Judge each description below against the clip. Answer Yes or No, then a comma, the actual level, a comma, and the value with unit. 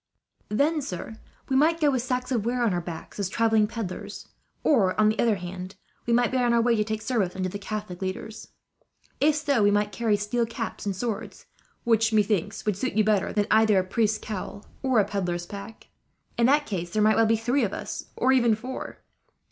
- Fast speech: Yes, fast, 215 wpm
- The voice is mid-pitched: No, high, 220 Hz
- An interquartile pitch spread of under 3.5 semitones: Yes, average, 3.1 semitones